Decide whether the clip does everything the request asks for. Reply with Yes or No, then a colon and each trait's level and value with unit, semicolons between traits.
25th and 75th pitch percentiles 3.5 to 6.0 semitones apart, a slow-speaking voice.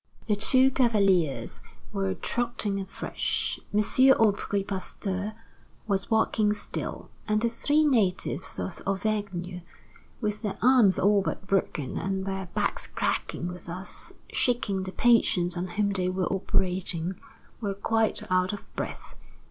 No: average, 2.8 semitones; slow, 130 wpm